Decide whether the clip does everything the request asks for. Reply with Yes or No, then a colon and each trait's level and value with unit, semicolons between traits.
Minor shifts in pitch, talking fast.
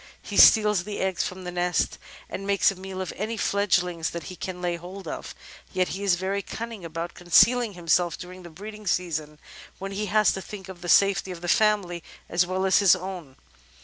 Yes: narrow, 2.2 semitones; fast, 210 wpm